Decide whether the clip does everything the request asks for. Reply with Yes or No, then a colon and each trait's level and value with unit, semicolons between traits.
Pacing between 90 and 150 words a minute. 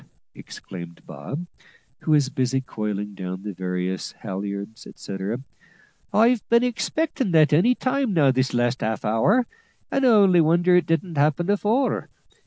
Yes: average, 140 wpm